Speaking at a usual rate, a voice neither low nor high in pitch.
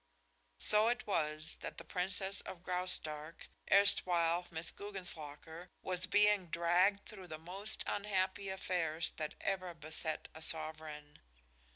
No: slow, 125 wpm; medium, 180 Hz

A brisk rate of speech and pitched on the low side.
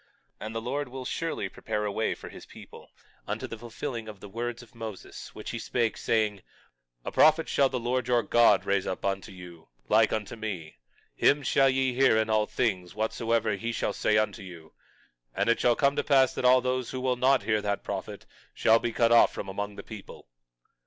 Yes: fast, 215 wpm; low, 115 Hz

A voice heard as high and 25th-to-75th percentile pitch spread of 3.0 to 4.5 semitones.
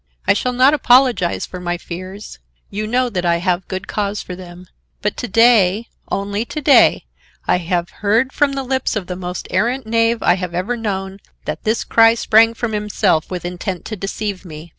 Yes: high, 205 Hz; average, 4.2 semitones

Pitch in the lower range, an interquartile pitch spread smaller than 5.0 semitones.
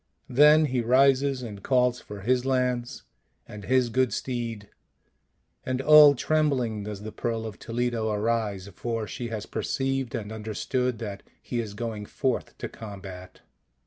Yes: low, 120 Hz; average, 3.3 semitones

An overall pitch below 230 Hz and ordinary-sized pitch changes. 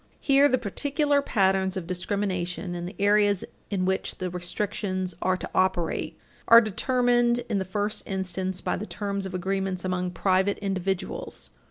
No: high, 190 Hz; narrow, 2.2 semitones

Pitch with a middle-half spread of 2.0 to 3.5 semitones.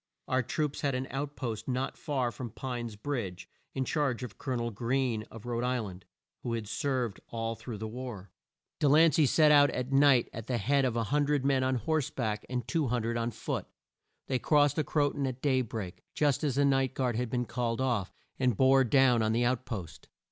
Yes: average, 3.0 semitones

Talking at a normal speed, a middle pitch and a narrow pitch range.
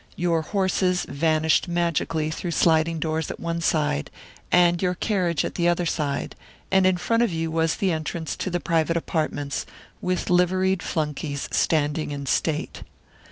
Yes: average, 160 wpm; medium, 165 Hz; narrow, 2.1 semitones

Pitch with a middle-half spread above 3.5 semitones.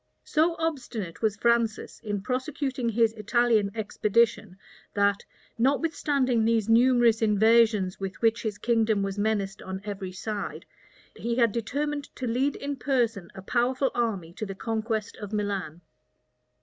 No: average, 3.0 semitones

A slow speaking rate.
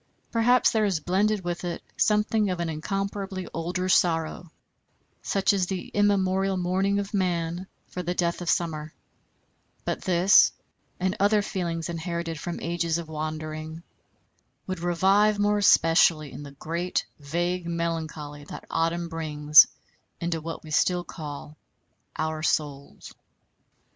Yes: slow, 130 wpm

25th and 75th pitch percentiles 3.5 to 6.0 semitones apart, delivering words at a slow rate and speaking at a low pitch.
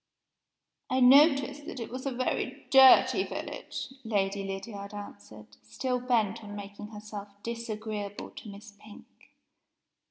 No: average, 3.8 semitones; slow, 125 wpm; high, 215 Hz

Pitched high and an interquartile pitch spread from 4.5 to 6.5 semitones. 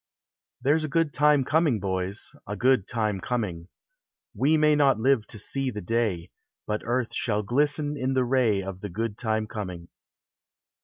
No: low, 115 Hz; average, 4.9 semitones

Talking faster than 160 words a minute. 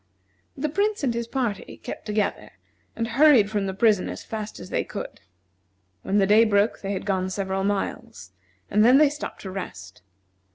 Yes: average, 180 wpm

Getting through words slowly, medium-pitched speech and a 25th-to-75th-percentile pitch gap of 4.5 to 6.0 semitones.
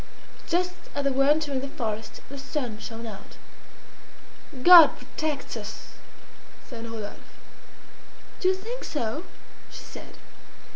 No: slow, 125 wpm; very high, 275 Hz; wide, 5.5 semitones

